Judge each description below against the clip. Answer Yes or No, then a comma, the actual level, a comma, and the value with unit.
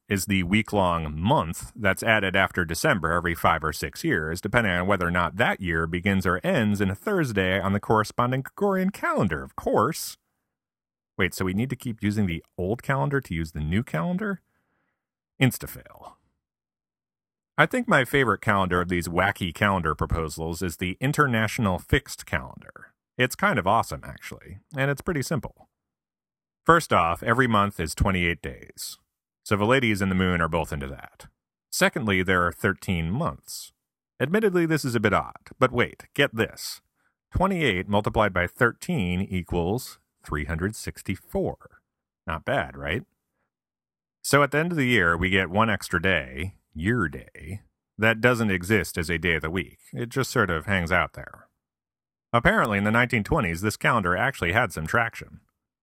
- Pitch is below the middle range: Yes, low, 100 Hz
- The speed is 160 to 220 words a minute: Yes, average, 165 wpm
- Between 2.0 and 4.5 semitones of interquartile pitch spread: No, average, 5.1 semitones